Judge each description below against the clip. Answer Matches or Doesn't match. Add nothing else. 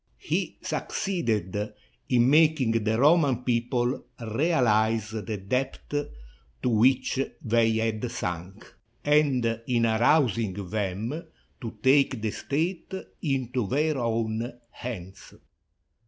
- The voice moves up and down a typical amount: Matches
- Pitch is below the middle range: Matches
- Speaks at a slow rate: Matches